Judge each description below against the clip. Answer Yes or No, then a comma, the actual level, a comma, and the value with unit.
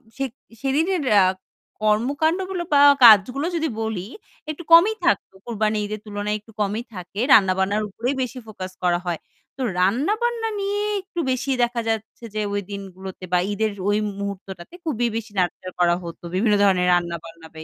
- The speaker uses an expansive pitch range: Yes, wide, 6.4 semitones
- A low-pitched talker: No, high, 215 Hz